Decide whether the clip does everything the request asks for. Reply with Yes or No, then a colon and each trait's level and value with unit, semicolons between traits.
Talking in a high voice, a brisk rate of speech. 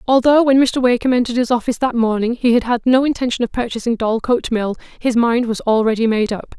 Yes: high, 240 Hz; fast, 220 wpm